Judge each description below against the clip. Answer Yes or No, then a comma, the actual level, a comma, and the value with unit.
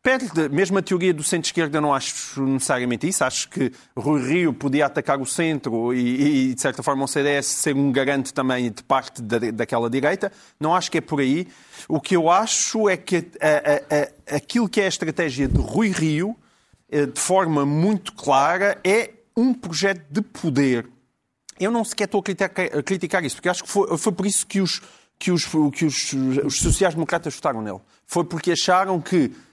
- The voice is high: No, medium, 160 Hz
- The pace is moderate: No, fast, 195 wpm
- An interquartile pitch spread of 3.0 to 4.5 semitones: No, wide, 5.6 semitones